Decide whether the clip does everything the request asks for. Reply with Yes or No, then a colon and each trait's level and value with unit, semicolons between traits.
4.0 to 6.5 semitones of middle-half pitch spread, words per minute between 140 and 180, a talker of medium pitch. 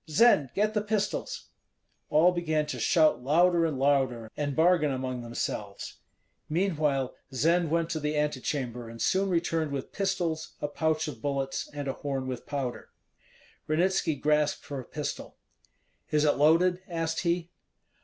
No: average, 3.6 semitones; average, 150 wpm; medium, 150 Hz